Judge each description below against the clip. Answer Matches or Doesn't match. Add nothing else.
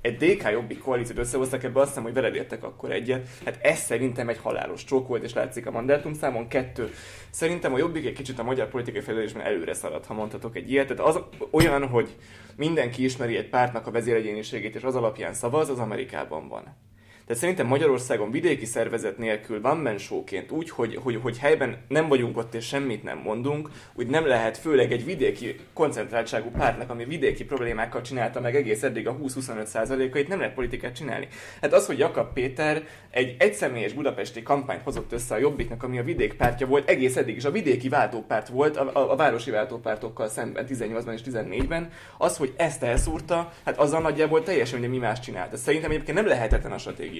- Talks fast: Matches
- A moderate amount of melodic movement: Matches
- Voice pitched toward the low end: Matches